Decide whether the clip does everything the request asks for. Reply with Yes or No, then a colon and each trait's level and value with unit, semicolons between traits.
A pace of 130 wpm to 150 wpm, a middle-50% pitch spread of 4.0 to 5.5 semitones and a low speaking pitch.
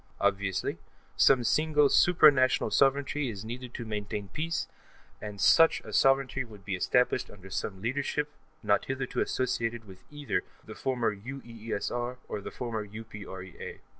Yes: average, 140 wpm; average, 4.7 semitones; low, 120 Hz